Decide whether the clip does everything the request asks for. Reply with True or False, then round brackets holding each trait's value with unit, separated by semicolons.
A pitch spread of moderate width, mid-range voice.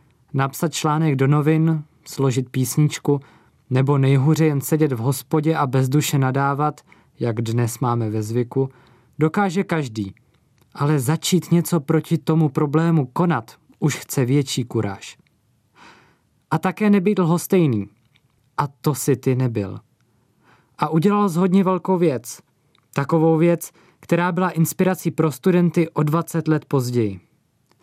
True (4.3 semitones; 150 Hz)